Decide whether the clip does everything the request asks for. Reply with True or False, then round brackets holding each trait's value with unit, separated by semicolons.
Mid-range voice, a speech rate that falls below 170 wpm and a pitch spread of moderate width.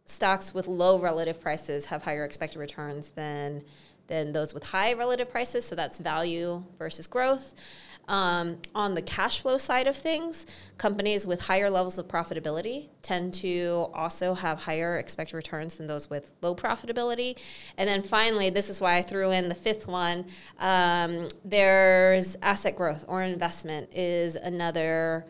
True (175 Hz; 160 wpm; 3.2 semitones)